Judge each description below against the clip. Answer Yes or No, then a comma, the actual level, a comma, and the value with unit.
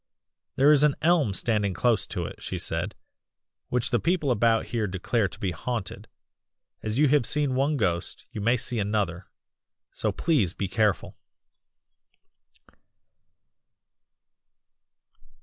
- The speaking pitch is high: No, low, 115 Hz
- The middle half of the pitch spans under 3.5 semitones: No, average, 5.2 semitones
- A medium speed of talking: No, slow, 130 wpm